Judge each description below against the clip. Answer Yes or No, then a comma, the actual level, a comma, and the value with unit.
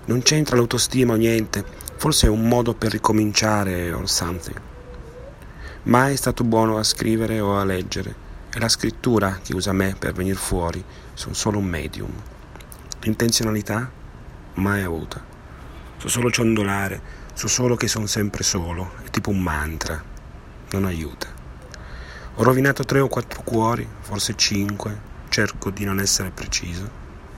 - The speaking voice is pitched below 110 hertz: Yes, low, 100 Hz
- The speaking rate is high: No, average, 145 wpm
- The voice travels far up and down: No, average, 3.8 semitones